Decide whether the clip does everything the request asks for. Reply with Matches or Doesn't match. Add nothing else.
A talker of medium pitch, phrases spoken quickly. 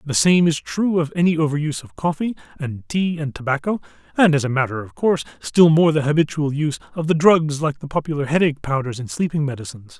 Matches